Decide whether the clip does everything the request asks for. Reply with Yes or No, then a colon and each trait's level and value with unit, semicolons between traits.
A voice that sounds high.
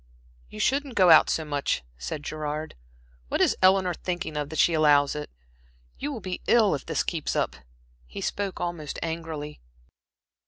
No: medium, 160 Hz